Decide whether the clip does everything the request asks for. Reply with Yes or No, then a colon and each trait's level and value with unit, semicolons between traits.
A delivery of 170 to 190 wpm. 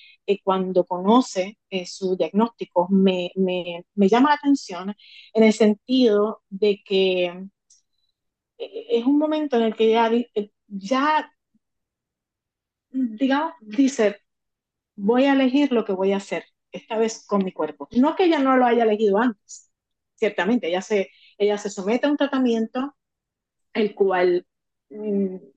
No: average, 140 wpm